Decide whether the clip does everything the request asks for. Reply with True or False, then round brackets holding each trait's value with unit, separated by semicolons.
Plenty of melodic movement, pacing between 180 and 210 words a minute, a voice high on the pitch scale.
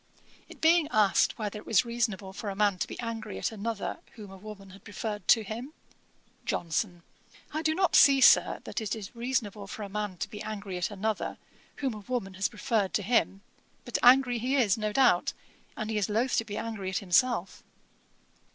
False (3.2 semitones; 200 wpm; 215 Hz)